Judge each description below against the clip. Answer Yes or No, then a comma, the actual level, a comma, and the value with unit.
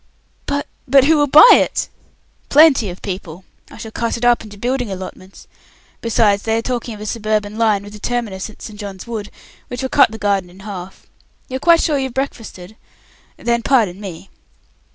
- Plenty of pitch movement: No, average, 3.7 semitones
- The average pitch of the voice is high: Yes, high, 220 Hz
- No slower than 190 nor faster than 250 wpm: Yes, average, 195 wpm